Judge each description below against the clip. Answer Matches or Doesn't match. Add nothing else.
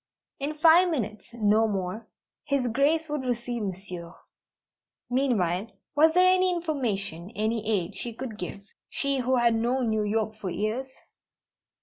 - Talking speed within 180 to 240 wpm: Doesn't match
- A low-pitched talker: Doesn't match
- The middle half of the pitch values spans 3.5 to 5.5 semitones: Matches